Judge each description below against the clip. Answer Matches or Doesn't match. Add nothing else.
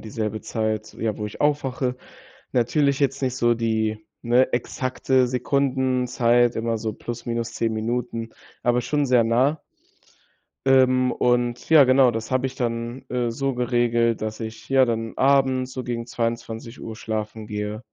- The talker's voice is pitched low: Matches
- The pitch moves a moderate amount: Doesn't match